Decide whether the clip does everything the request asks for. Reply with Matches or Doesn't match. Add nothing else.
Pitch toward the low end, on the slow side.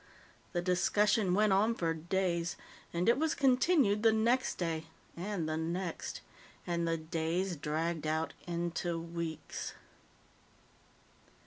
Doesn't match